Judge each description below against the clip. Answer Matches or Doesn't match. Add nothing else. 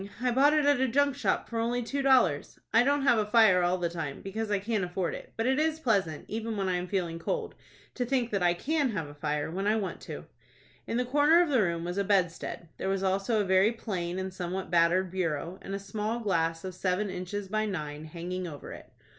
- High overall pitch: Matches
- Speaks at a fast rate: Matches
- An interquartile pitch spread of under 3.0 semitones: Doesn't match